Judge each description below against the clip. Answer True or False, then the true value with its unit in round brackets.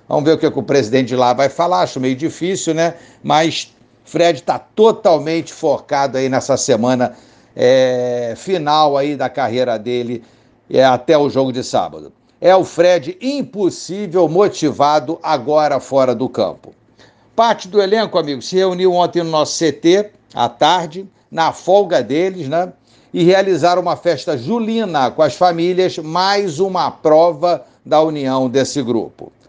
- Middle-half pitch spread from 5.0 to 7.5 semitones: True (5.3 semitones)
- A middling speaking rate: True (155 wpm)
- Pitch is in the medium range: True (160 Hz)